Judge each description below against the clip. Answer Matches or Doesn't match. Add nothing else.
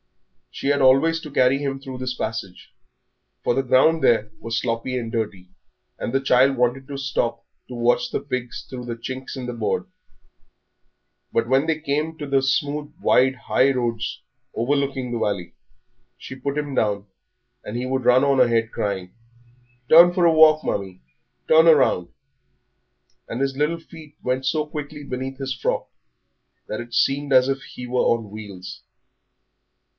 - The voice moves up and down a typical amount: Matches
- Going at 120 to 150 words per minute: Doesn't match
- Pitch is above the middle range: Doesn't match